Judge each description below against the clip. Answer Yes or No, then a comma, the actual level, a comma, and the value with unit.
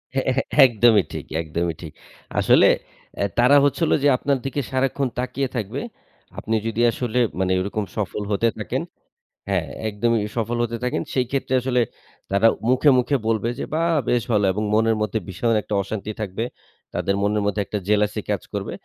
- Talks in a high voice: No, low, 115 Hz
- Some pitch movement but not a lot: Yes, average, 3.4 semitones